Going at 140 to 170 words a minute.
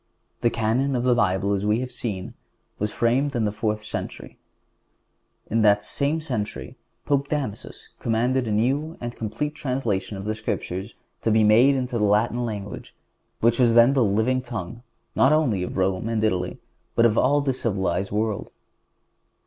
Yes: average, 165 wpm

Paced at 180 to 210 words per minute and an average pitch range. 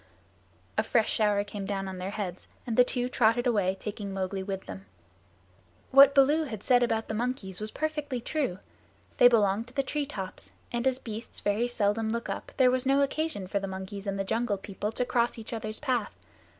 Yes: average, 200 wpm; average, 4.1 semitones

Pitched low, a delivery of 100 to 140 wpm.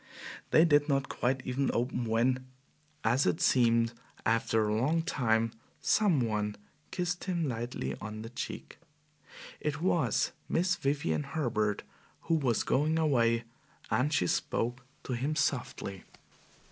Yes: low, 125 Hz; slow, 135 wpm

